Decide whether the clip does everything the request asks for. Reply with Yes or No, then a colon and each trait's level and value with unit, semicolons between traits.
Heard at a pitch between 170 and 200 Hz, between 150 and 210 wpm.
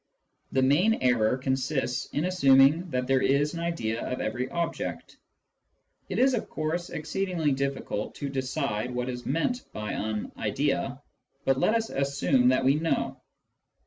No: low, 135 Hz; average, 160 wpm